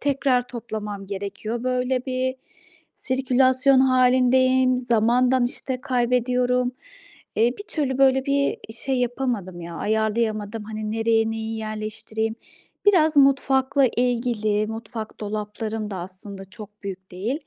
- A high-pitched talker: Yes, high, 240 Hz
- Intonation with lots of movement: No, average, 3.3 semitones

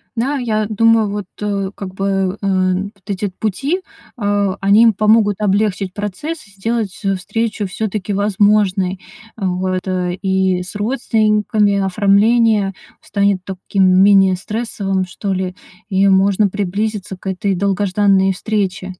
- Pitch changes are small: Yes, narrow, 2.0 semitones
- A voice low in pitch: No, high, 200 Hz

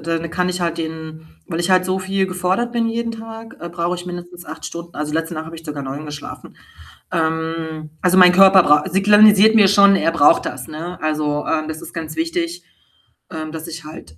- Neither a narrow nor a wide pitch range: Yes, average, 3.2 semitones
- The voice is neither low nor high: Yes, medium, 170 Hz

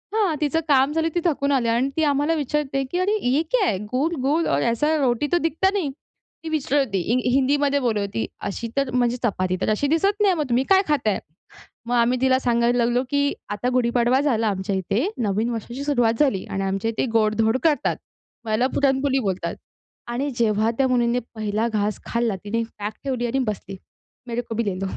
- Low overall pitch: No, very high, 250 Hz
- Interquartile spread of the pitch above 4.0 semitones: Yes, average, 4.4 semitones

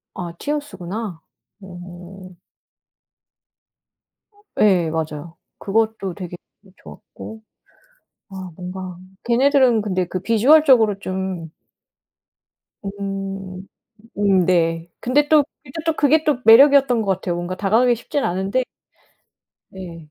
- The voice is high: Yes, high, 195 Hz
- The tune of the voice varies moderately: Yes, average, 4.8 semitones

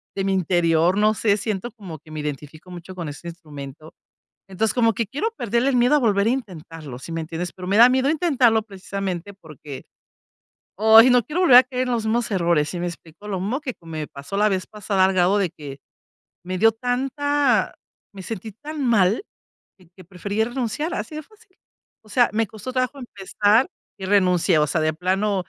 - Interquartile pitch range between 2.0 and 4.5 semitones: No, wide, 5.6 semitones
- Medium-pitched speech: No, high, 200 Hz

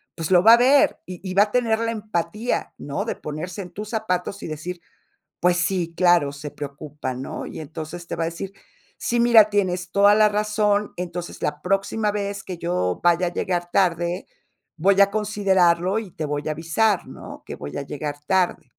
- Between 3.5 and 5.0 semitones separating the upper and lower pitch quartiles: Yes, average, 3.8 semitones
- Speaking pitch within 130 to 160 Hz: No, medium, 180 Hz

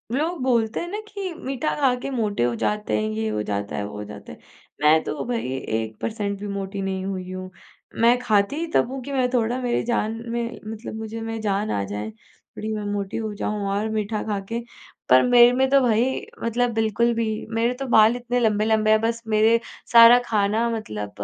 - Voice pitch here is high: Yes, high, 220 Hz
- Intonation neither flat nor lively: Yes, average, 3.3 semitones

